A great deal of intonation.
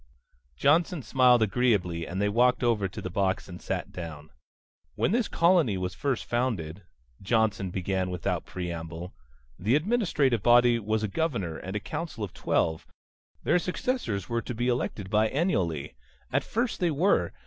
Yes: wide, 6.4 semitones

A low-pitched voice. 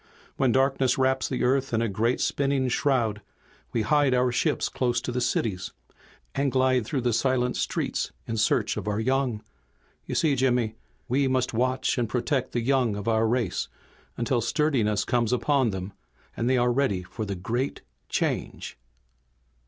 Yes: low, 125 Hz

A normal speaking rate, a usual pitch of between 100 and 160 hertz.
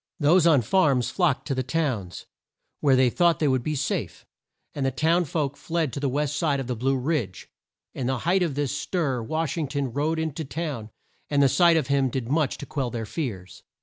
No: fast, 220 wpm; medium, 140 Hz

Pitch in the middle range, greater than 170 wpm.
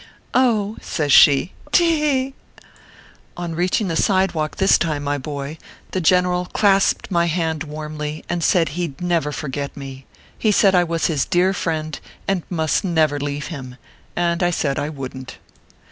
Yes: medium, 165 Hz; average, 180 wpm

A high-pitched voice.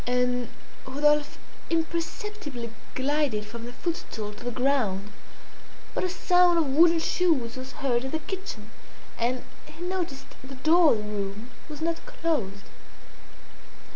Yes: very high, 275 Hz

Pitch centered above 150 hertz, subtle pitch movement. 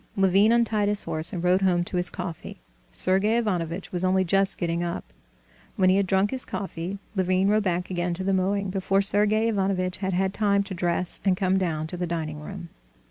Yes: high, 190 Hz; narrow, 2.0 semitones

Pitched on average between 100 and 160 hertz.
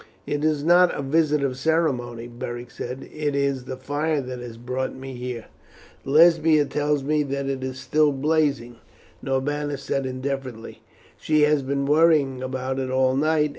Yes: medium, 140 Hz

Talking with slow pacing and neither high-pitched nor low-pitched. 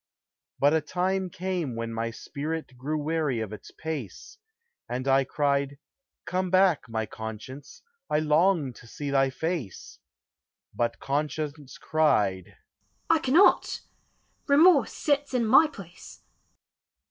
Yes: slow, 125 wpm; medium, 150 Hz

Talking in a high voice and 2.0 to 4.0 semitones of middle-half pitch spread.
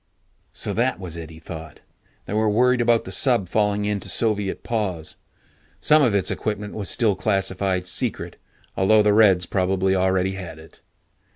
No: low, 100 Hz; average, 2.8 semitones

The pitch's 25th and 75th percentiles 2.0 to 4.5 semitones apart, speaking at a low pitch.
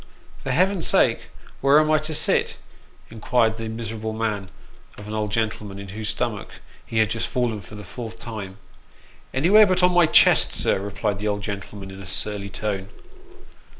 Yes: average, 3.5 semitones; low, 110 Hz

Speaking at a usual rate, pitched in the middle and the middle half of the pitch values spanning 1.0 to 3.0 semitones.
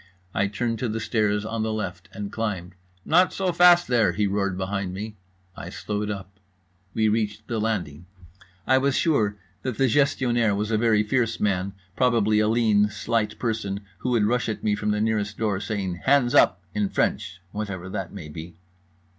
No: average, 180 wpm; low, 105 Hz; narrow, 2.5 semitones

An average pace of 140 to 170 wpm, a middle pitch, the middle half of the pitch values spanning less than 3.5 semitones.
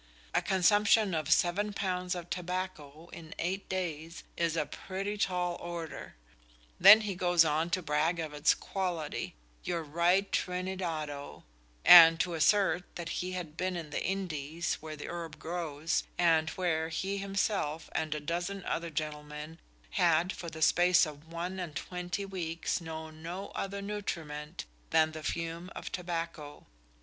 Yes: average, 150 wpm; medium, 170 Hz; narrow, 2.6 semitones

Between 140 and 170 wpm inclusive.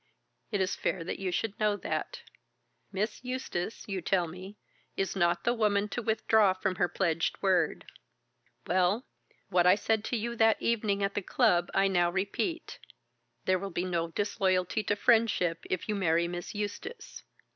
Yes: average, 165 wpm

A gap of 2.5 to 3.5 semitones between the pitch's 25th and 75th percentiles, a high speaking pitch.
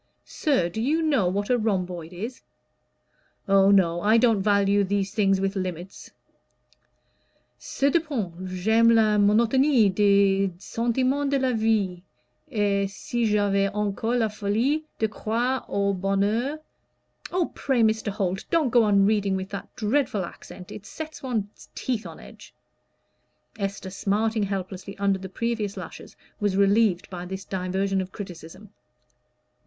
Yes: average, 3.0 semitones; high, 205 Hz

